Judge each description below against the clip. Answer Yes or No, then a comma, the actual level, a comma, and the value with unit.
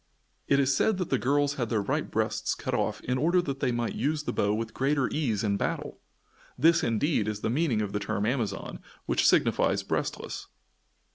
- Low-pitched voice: Yes, low, 130 Hz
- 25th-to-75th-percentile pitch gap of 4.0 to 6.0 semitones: Yes, average, 5.2 semitones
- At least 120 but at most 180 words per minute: No, average, 200 wpm